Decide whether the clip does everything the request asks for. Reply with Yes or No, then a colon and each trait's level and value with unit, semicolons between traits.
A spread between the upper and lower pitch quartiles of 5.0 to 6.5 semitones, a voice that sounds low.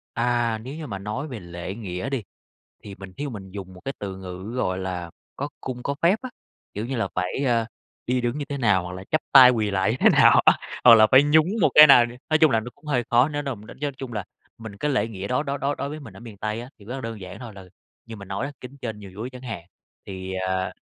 Yes: wide, 5.5 semitones; low, 115 Hz